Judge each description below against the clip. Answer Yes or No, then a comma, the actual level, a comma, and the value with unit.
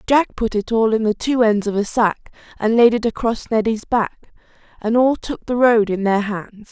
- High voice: Yes, high, 225 Hz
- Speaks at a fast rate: Yes, fast, 225 wpm